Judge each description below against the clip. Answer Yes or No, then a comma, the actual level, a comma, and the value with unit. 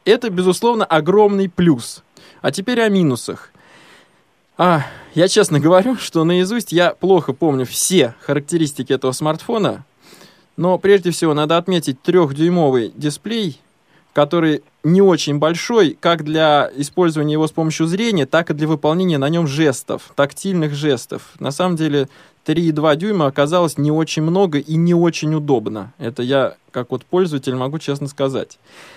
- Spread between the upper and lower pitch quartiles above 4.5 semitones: No, average, 4.0 semitones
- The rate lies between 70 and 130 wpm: No, average, 145 wpm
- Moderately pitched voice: Yes, medium, 160 Hz